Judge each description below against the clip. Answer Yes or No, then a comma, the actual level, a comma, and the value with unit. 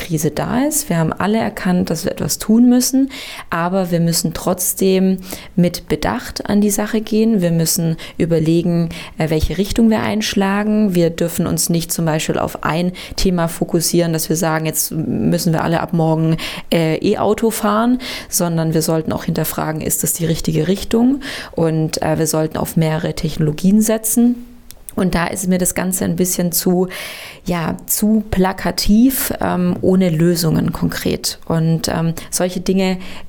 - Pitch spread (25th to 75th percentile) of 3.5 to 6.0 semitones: Yes, average, 4.1 semitones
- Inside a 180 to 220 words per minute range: No, average, 160 wpm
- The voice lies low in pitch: No, medium, 180 Hz